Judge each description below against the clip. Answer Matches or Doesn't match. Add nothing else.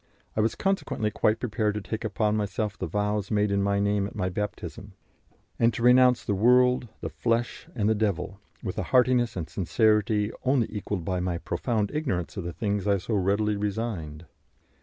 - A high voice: Doesn't match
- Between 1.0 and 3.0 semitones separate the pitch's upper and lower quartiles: Matches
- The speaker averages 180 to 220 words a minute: Matches